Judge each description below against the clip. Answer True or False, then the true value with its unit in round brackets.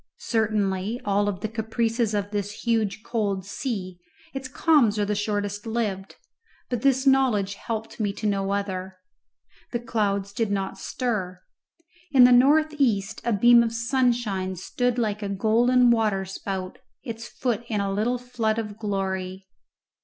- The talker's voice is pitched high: True (215 Hz)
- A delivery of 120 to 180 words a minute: True (150 wpm)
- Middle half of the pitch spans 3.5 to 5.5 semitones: False (3.1 semitones)